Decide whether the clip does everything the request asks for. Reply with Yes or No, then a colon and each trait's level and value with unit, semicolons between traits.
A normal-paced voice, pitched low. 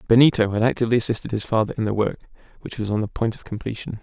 No: fast, 240 wpm; low, 110 Hz